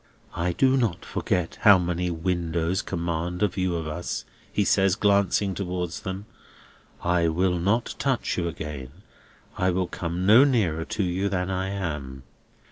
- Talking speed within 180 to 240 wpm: No, average, 155 wpm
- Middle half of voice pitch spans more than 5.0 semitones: No, average, 2.7 semitones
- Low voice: Yes, very low, 90 Hz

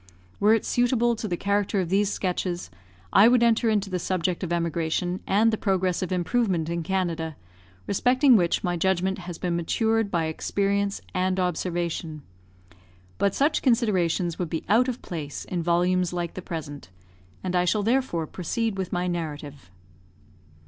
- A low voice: No, medium, 185 Hz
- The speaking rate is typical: Yes, average, 160 wpm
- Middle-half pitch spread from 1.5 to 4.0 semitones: Yes, average, 3.3 semitones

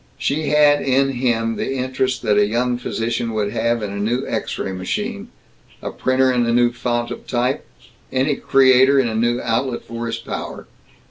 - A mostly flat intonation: Yes, narrow, 2.3 semitones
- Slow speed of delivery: No, average, 190 wpm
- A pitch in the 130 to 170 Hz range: No, low, 120 Hz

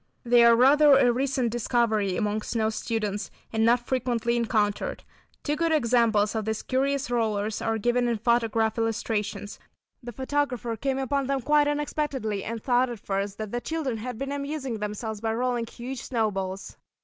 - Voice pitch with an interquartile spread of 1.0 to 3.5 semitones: Yes, average, 3.2 semitones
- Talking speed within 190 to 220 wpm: No, average, 165 wpm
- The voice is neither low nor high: No, high, 235 Hz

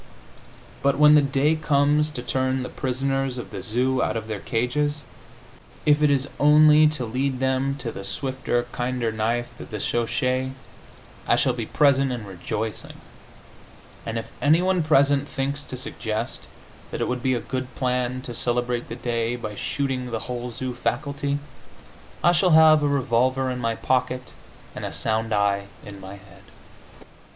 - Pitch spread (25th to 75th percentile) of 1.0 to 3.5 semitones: Yes, average, 3.1 semitones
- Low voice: Yes, low, 130 Hz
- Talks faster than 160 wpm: Yes, average, 170 wpm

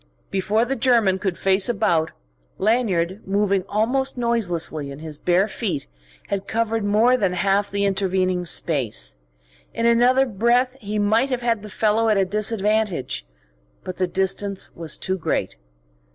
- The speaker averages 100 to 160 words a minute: Yes, average, 150 wpm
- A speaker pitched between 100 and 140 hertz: No, high, 200 Hz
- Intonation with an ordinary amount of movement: Yes, average, 3.6 semitones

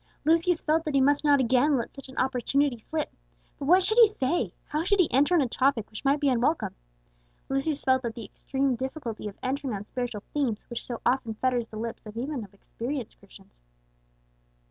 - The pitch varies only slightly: No, average, 3.9 semitones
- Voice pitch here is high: Yes, very high, 265 Hz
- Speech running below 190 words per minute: No, average, 195 wpm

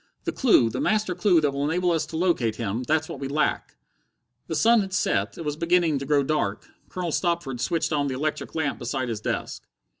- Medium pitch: Yes, medium, 150 Hz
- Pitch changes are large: No, average, 4.4 semitones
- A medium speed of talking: No, fast, 215 wpm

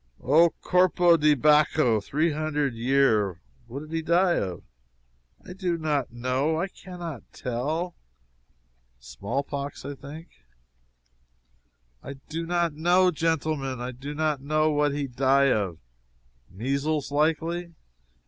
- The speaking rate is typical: No, slow, 125 wpm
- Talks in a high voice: No, medium, 150 Hz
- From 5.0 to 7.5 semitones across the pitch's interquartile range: No, average, 3.6 semitones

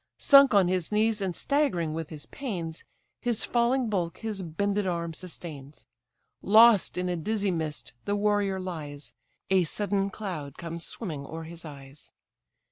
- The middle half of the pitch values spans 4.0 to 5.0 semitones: Yes, average, 4.3 semitones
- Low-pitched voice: No, medium, 185 Hz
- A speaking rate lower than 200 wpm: Yes, average, 150 wpm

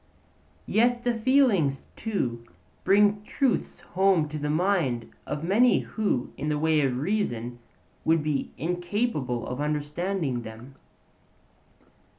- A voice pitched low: No, medium, 160 Hz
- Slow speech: Yes, slow, 120 wpm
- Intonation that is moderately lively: No, wide, 7.0 semitones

